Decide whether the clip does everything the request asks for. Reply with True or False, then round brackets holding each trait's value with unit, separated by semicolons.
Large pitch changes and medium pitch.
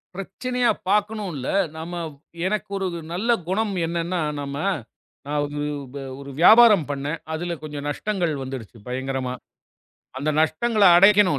True (6.4 semitones; 175 Hz)